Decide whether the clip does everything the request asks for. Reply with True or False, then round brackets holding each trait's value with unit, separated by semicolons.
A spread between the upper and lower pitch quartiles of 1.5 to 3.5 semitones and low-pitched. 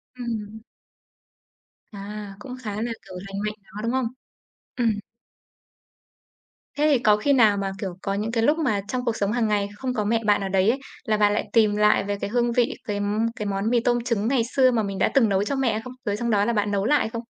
False (2.8 semitones; 215 Hz)